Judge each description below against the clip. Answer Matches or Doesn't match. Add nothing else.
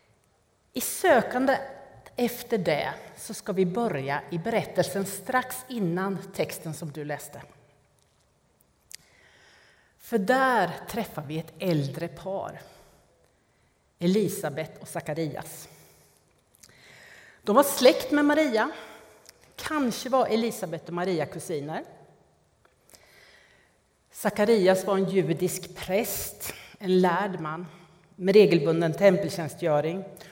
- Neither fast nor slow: Doesn't match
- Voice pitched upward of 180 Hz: Matches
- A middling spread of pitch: Matches